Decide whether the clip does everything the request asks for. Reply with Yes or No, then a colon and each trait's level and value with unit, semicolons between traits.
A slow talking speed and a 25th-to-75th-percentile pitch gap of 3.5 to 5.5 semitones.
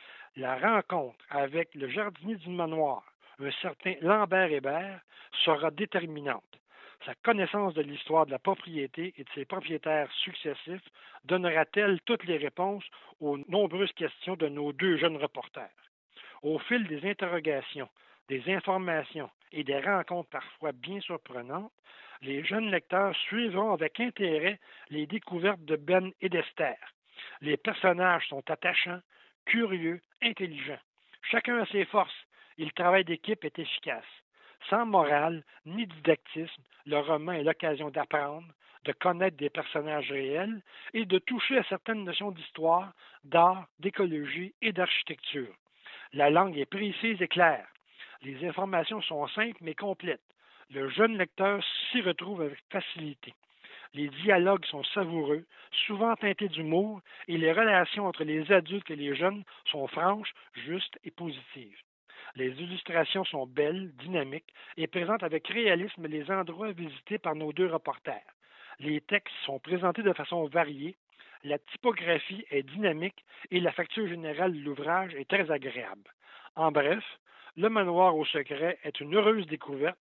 Yes: slow, 140 wpm; average, 4.3 semitones